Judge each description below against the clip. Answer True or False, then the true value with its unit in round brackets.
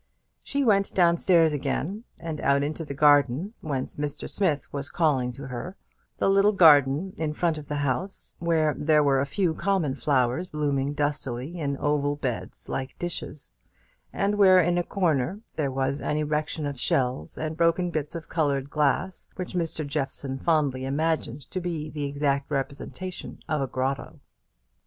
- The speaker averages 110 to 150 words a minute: False (165 wpm)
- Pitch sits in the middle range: True (150 Hz)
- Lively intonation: False (3.5 semitones)